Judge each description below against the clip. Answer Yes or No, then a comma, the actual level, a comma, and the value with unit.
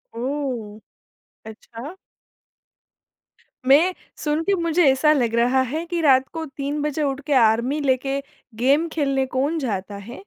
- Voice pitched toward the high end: Yes, very high, 275 Hz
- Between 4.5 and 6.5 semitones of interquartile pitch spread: No, average, 3.7 semitones